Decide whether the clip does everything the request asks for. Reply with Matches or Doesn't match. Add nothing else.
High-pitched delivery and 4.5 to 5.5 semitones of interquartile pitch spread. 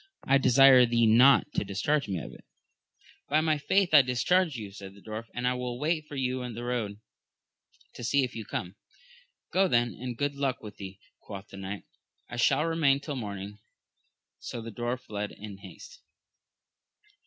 Doesn't match